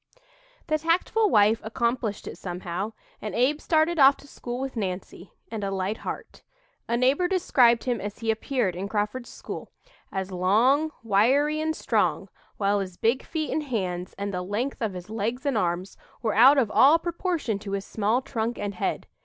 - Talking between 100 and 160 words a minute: No, average, 180 wpm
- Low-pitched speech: No, high, 225 Hz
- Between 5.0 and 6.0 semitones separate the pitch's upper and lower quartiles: Yes, wide, 5.6 semitones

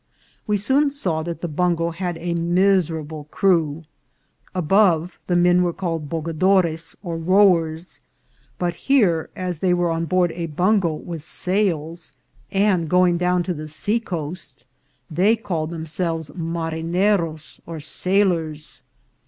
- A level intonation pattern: Yes, narrow, 2.3 semitones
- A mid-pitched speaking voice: Yes, medium, 170 Hz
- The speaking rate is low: Yes, slow, 130 wpm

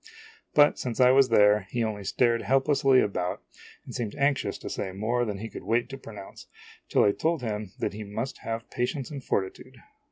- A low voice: Yes, low, 115 Hz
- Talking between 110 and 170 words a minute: No, average, 195 wpm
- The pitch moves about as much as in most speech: Yes, average, 4.3 semitones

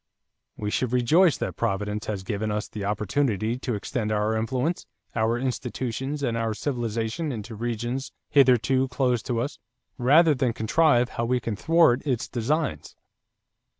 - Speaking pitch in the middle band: No, low, 120 Hz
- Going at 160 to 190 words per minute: No, average, 150 wpm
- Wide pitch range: No, average, 3.4 semitones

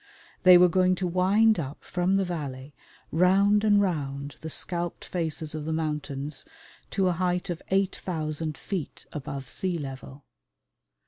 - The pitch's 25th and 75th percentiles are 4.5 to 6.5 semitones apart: No, average, 3.7 semitones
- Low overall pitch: No, medium, 170 Hz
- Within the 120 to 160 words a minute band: Yes, average, 145 wpm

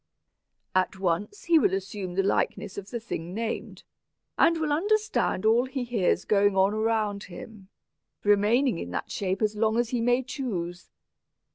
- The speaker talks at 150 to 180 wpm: Yes, average, 160 wpm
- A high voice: Yes, high, 215 Hz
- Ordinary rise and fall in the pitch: Yes, average, 4.2 semitones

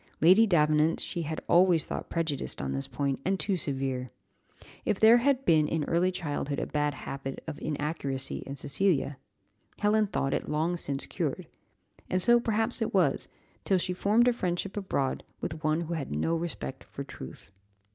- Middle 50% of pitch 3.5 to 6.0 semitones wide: Yes, average, 5.2 semitones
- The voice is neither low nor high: Yes, medium, 160 Hz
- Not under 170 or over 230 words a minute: Yes, average, 175 wpm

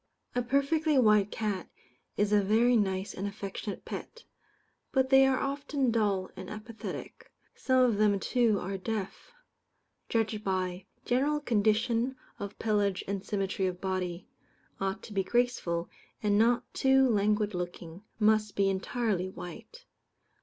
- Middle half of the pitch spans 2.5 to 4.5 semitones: Yes, average, 3.9 semitones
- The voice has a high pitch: Yes, high, 210 Hz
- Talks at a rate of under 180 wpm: Yes, average, 140 wpm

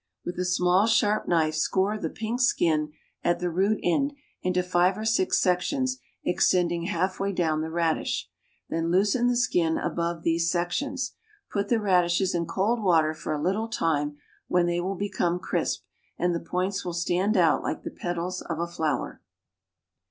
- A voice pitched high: No, medium, 180 Hz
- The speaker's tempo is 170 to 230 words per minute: Yes, average, 175 wpm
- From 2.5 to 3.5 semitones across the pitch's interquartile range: Yes, average, 3.0 semitones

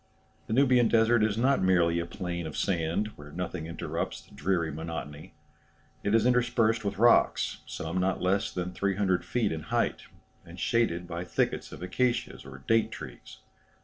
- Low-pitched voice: Yes, very low, 95 Hz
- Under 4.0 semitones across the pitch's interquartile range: No, average, 5.1 semitones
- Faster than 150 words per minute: Yes, average, 165 wpm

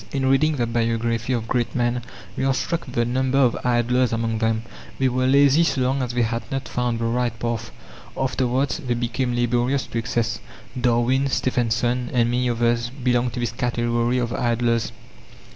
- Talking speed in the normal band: Yes, average, 180 wpm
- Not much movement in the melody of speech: Yes, narrow, 1.6 semitones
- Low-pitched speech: Yes, low, 120 Hz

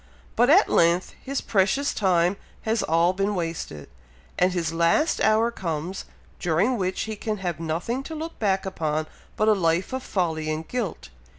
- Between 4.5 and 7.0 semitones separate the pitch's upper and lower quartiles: Yes, average, 4.8 semitones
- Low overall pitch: No, medium, 185 Hz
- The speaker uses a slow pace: No, average, 170 wpm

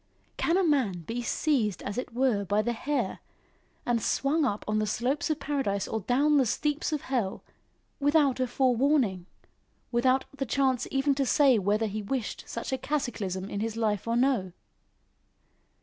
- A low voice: No, high, 245 Hz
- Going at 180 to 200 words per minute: No, average, 170 wpm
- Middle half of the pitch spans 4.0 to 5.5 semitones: Yes, average, 4.7 semitones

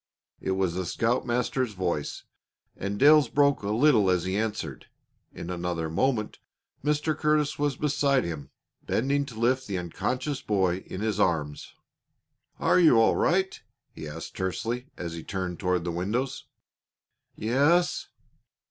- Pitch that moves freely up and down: Yes, wide, 7.2 semitones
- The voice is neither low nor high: No, low, 110 Hz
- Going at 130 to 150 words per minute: Yes, average, 140 wpm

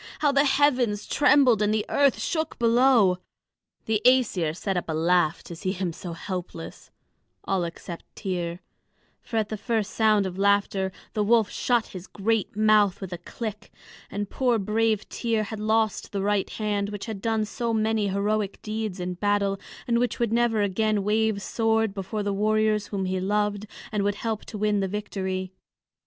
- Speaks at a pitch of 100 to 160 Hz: No, high, 210 Hz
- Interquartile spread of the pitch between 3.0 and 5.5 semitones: No, narrow, 2.4 semitones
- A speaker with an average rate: Yes, average, 175 wpm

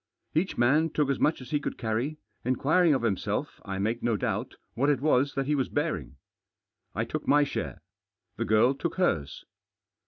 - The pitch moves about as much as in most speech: Yes, average, 4.4 semitones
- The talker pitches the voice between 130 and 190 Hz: Yes, low, 135 Hz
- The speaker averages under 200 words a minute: Yes, average, 185 wpm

